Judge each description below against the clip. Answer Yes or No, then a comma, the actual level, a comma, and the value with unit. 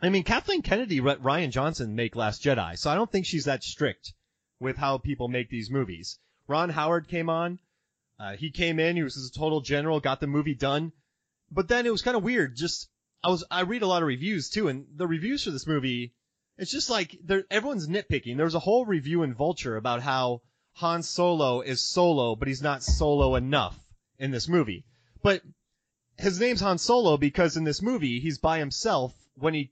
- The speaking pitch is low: No, medium, 150 Hz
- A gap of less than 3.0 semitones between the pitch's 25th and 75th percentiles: No, average, 5.3 semitones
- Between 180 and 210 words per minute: Yes, average, 200 wpm